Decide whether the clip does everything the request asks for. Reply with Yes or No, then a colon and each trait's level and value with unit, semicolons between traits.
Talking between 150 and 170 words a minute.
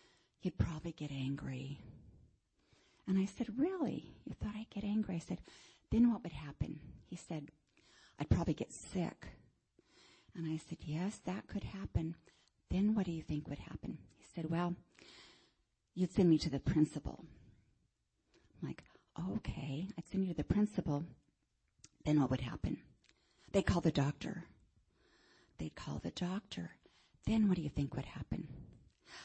Yes: average, 155 wpm